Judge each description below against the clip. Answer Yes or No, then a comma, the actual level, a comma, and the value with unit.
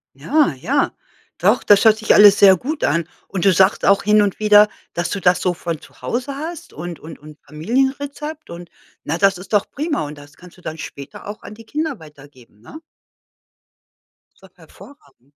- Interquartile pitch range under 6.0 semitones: No, wide, 7.4 semitones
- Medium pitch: No, high, 195 Hz